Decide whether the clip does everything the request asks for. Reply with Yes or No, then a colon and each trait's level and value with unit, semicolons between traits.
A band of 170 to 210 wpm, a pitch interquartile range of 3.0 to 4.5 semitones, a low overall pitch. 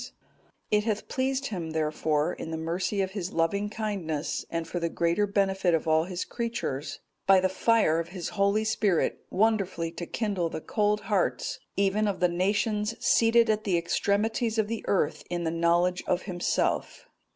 No: average, 175 wpm; average, 4.0 semitones; high, 190 Hz